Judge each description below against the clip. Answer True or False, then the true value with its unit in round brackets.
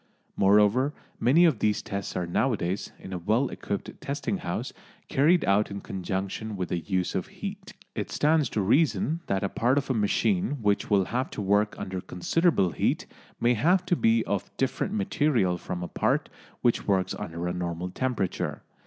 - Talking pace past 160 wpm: True (180 wpm)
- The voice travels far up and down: True (6.3 semitones)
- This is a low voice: True (105 Hz)